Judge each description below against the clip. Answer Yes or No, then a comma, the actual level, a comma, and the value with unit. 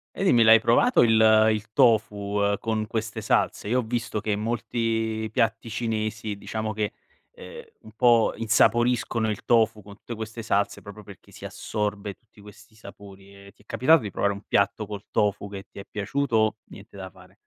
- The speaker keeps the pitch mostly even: Yes, narrow, 1.9 semitones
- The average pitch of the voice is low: Yes, low, 110 Hz